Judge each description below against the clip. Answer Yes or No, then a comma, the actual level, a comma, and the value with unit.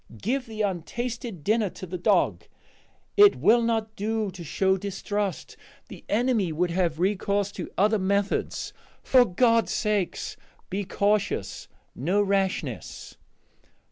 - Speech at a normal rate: No, slow, 125 wpm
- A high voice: Yes, high, 205 Hz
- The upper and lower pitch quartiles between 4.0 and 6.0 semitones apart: No, average, 3.0 semitones